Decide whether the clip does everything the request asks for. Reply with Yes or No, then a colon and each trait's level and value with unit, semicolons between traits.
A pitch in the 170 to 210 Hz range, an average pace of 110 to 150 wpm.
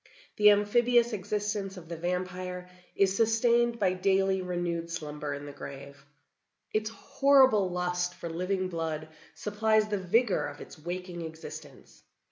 Yes: medium, 185 Hz; slow, 135 wpm